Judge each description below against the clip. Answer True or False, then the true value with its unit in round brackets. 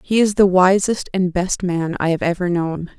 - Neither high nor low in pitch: True (180 Hz)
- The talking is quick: True (220 wpm)